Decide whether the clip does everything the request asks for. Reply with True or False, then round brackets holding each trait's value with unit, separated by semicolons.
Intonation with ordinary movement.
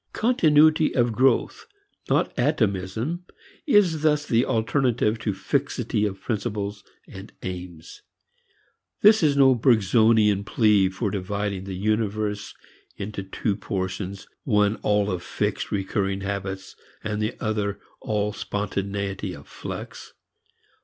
True (3.5 semitones)